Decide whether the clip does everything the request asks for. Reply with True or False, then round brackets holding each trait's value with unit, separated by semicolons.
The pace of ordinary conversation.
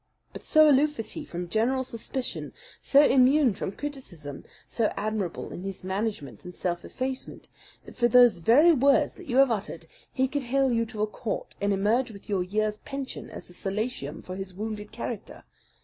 True (185 wpm)